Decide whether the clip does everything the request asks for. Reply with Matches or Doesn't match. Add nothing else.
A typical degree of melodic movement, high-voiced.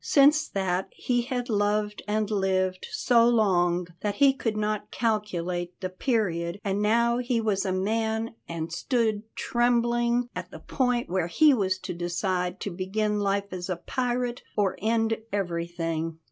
Matches